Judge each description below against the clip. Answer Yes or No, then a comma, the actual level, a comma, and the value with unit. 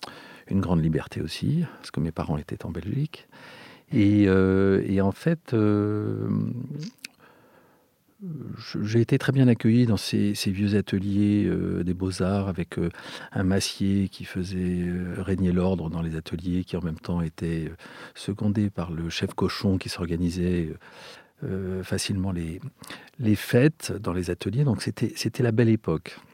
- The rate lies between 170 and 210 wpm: No, average, 155 wpm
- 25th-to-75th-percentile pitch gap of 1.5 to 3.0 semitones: No, average, 3.7 semitones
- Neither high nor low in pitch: No, very low, 95 Hz